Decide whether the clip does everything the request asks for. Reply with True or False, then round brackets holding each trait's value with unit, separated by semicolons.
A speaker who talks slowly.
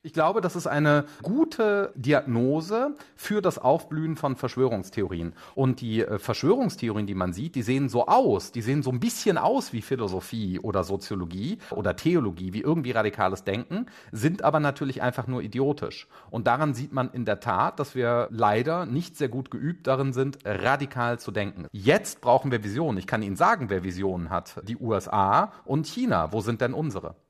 False (180 wpm)